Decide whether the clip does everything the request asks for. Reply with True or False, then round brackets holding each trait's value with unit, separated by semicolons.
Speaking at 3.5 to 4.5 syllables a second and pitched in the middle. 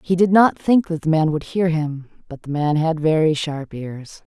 True (4.4 syllables/s; 160 Hz)